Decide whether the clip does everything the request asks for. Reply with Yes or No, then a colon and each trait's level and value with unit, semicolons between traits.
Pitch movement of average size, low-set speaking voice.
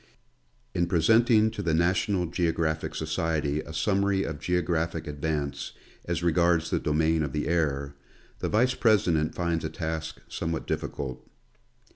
No: narrow, 2.3 semitones; very low, 80 Hz